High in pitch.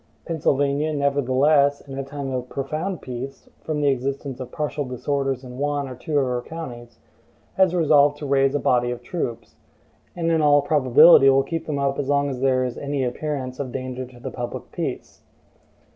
No: medium, 140 Hz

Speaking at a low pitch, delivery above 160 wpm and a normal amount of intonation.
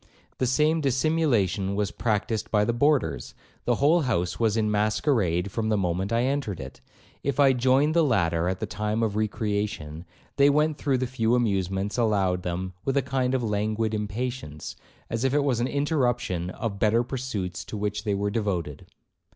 Yes: low, 110 Hz; average, 180 wpm; average, 4.6 semitones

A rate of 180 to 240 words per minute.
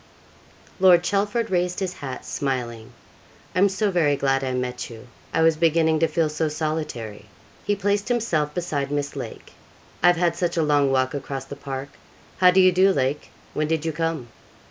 Yes: average, 185 wpm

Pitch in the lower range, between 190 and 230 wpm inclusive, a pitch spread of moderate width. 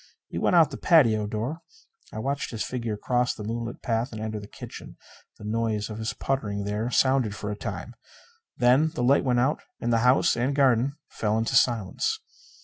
Yes: low, 115 Hz; average, 195 wpm; average, 3.3 semitones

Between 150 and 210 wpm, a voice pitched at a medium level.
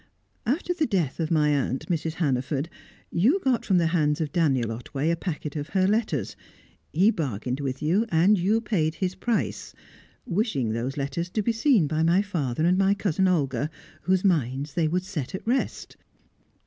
Yes: average, 180 wpm; medium, 165 Hz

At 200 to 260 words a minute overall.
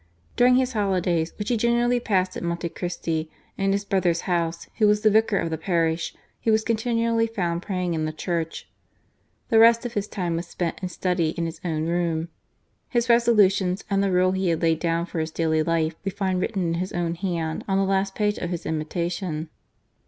Yes: fast, 205 wpm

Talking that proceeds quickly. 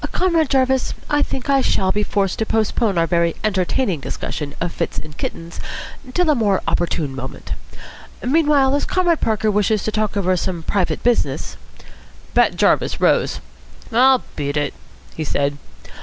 No: average, 160 wpm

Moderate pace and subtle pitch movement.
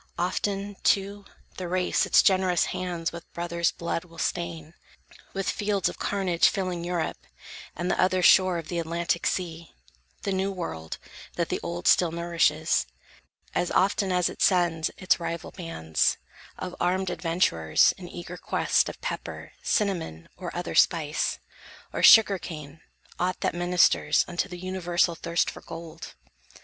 Yes: average, 150 wpm; narrow, 1.8 semitones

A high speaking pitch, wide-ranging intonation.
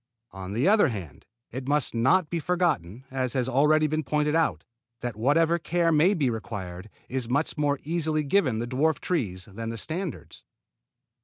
No: medium, 140 Hz; wide, 5.8 semitones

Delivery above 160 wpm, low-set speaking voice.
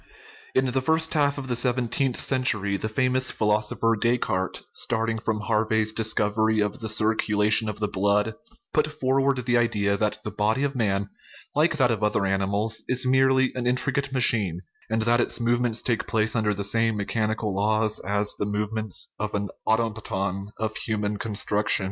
Yes: average, 170 wpm; low, 110 Hz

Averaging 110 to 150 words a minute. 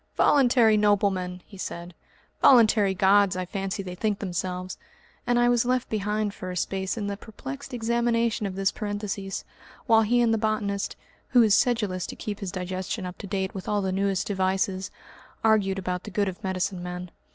No: average, 185 wpm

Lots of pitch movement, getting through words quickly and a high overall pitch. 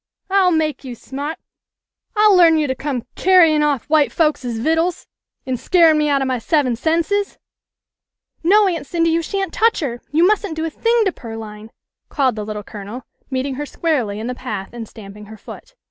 Yes: wide, 5.7 semitones; fast, 210 wpm; very high, 300 Hz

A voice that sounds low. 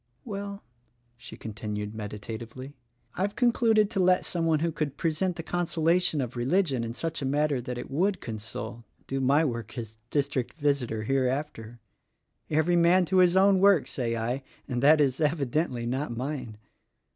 No: medium, 145 Hz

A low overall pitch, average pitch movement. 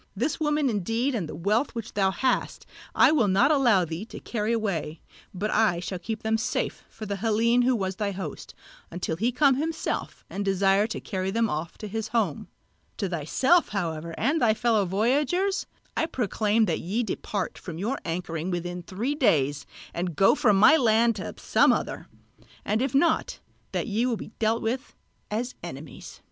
No: high, 215 Hz; average, 4.5 semitones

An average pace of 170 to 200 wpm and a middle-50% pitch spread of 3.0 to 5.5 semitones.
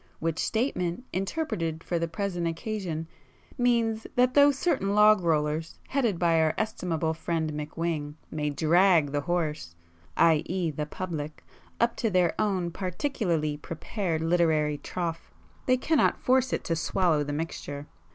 No: slow, 135 wpm; average, 4.7 semitones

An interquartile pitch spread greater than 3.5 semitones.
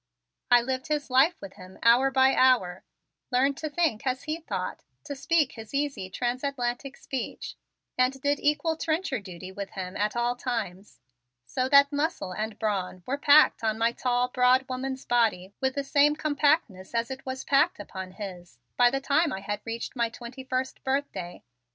Yes: average, 4.5 semitones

